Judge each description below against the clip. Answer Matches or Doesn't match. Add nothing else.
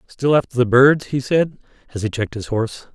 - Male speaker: Matches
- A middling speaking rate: Doesn't match